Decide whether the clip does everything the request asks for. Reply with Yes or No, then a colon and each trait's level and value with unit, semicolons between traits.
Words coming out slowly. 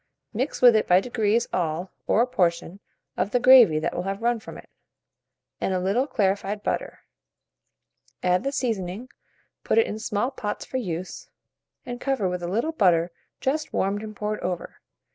No: average, 175 wpm